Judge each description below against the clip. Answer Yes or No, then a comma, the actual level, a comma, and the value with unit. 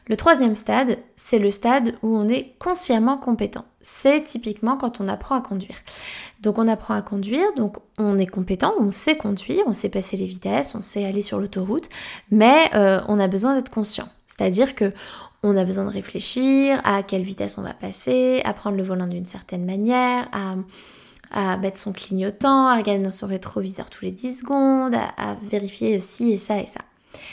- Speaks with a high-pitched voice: Yes, high, 215 Hz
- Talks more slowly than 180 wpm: No, average, 195 wpm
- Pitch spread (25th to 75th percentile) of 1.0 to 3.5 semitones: No, average, 4.2 semitones